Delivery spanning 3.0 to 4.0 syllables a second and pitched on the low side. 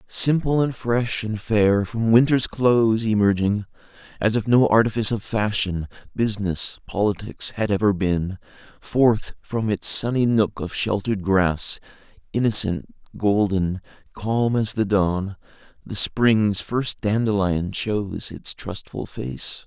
Yes: 3.9 syllables/s; low, 105 Hz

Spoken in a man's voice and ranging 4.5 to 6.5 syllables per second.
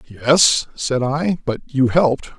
No: male; 4.2 syllables/s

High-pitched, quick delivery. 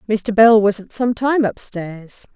No: high, 215 Hz; average, 180 wpm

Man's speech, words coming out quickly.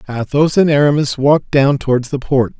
No: male; average, 185 wpm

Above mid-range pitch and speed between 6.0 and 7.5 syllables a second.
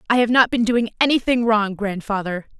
No: high, 220 Hz; 5.4 syllables/s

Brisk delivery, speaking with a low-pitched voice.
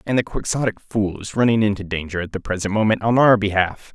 Yes: fast, 230 wpm; low, 105 Hz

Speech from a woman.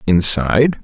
No: male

